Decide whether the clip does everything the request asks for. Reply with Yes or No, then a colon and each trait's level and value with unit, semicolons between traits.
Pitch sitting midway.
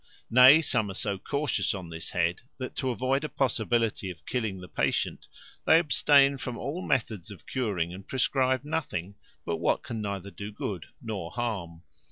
No: low, 110 Hz